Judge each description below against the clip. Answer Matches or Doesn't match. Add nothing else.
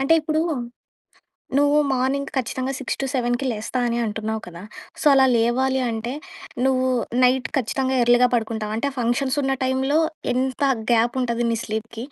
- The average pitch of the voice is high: Matches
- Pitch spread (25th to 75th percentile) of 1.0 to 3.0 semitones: Matches